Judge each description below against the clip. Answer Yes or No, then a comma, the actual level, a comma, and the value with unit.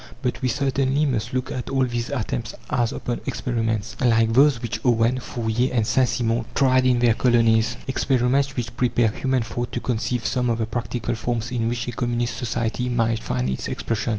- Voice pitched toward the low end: Yes, low, 120 Hz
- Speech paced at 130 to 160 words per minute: No, average, 190 wpm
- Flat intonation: Yes, narrow, 1.9 semitones